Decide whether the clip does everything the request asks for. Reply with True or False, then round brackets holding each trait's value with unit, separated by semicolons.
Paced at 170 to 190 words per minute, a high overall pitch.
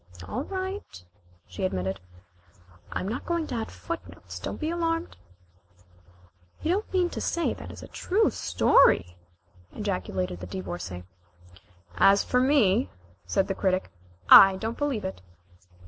False (140 wpm; 220 Hz)